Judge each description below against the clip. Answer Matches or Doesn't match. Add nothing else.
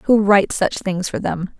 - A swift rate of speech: Matches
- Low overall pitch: Doesn't match